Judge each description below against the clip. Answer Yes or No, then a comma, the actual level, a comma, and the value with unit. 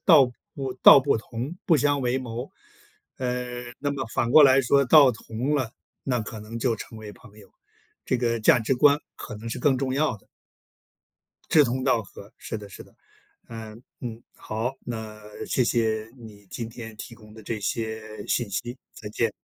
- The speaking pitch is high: No, low, 120 Hz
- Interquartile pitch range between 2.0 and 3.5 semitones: Yes, average, 3.0 semitones